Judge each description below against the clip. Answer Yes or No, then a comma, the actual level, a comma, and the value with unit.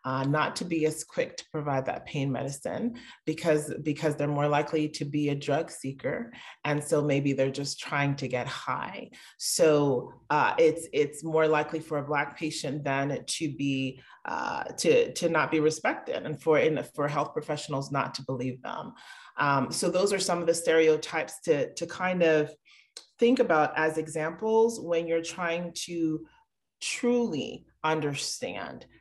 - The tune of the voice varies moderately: Yes, average, 3.0 semitones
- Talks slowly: No, average, 170 wpm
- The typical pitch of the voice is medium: Yes, medium, 155 Hz